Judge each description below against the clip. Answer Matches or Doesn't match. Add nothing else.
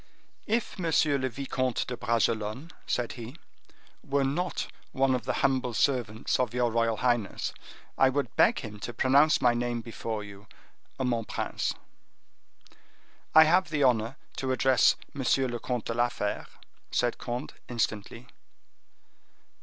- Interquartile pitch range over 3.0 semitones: Doesn't match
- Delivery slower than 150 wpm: Matches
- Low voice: Matches